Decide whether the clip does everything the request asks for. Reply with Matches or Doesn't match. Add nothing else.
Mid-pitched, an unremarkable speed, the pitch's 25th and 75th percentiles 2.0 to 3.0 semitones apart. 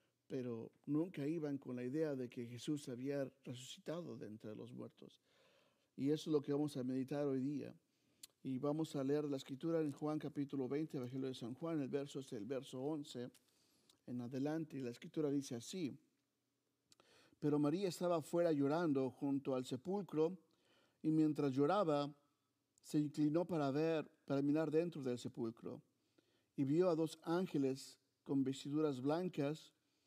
Matches